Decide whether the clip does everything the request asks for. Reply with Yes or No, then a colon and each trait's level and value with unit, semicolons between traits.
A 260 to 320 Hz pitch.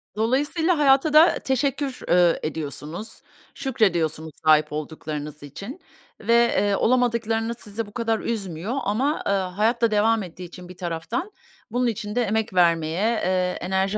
No: high, 210 Hz